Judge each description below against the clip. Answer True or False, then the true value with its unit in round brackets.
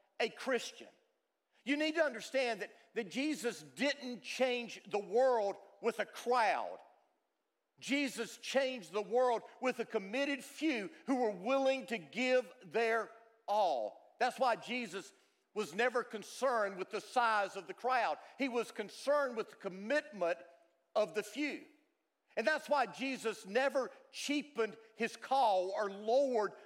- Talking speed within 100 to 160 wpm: True (140 wpm)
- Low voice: False (235 Hz)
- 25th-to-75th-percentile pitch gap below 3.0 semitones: False (4.1 semitones)